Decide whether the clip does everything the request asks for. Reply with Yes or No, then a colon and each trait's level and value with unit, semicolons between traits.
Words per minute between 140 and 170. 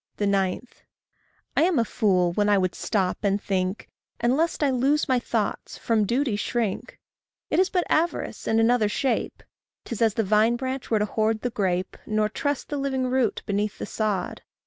No: average, 185 wpm